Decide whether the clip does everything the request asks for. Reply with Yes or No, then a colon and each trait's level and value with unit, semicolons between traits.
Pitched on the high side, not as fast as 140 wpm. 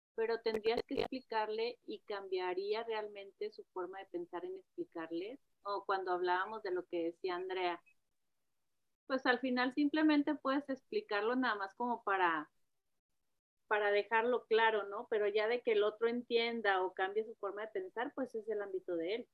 No: high, 215 Hz; average, 170 wpm